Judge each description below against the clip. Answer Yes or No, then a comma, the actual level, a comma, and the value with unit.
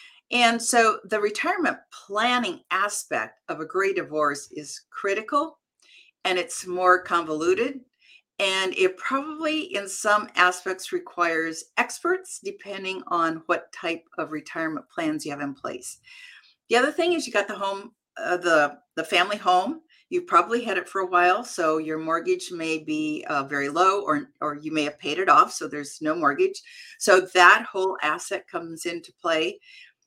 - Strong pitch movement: Yes, wide, 8.6 semitones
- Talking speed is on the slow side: No, average, 165 wpm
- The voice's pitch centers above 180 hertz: Yes, high, 190 Hz